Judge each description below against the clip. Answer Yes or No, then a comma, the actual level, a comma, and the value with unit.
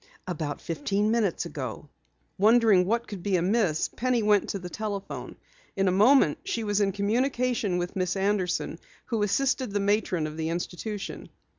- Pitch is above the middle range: Yes, high, 200 Hz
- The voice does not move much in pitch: No, average, 3.6 semitones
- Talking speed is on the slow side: No, average, 160 wpm